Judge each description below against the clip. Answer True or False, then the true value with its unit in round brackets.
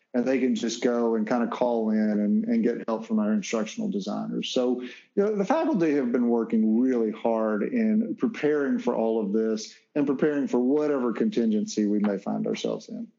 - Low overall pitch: True (125 Hz)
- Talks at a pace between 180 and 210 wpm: True (200 wpm)